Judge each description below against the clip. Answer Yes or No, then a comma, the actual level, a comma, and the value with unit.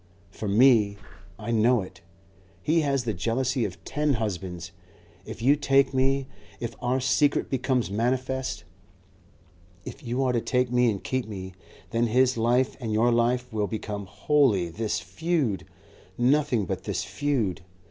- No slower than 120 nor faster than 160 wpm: Yes, average, 150 wpm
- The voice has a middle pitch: No, low, 120 Hz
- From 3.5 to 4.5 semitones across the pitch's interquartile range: Yes, average, 3.9 semitones